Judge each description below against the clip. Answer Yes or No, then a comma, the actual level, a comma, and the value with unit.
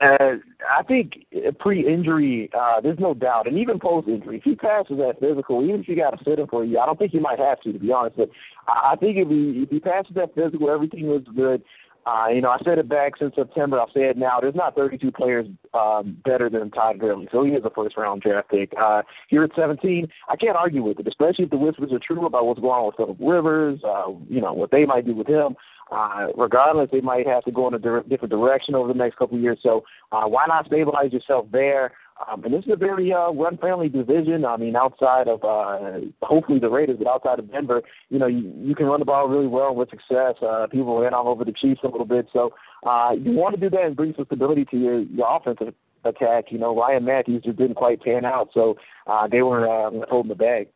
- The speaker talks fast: Yes, fast, 250 wpm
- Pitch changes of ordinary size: Yes, average, 4.5 semitones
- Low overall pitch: Yes, low, 130 Hz